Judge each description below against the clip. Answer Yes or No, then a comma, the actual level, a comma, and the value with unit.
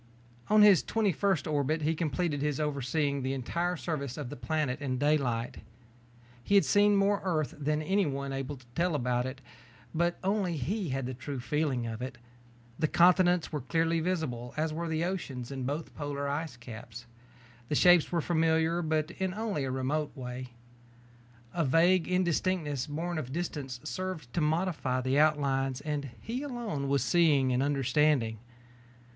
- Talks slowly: No, average, 165 wpm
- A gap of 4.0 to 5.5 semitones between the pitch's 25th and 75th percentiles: Yes, average, 4.4 semitones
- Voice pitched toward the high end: No, medium, 150 Hz